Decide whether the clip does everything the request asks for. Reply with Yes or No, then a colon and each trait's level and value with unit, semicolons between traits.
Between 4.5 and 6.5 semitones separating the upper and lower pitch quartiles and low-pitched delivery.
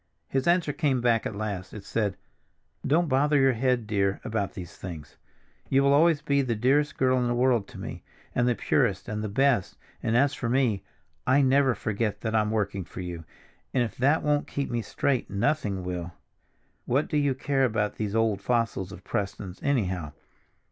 Yes: average, 5.1 semitones; low, 120 Hz